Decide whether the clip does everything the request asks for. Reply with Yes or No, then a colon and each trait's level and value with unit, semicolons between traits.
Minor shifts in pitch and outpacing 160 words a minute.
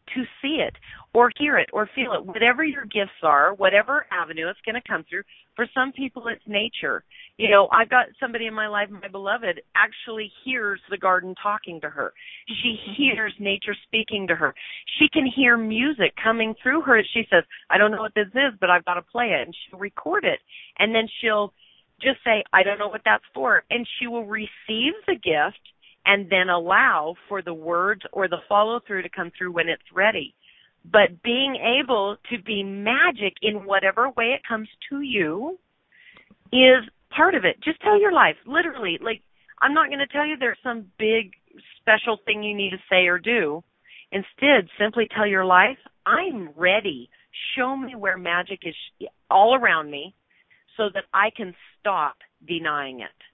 No: average, 4.4 semitones; average, 190 wpm